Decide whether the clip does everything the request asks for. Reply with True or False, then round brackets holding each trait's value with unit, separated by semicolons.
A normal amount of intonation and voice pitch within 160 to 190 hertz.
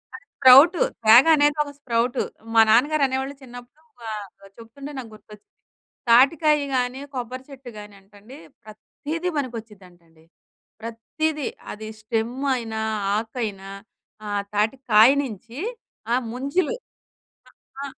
False (4.1 semitones; 245 Hz)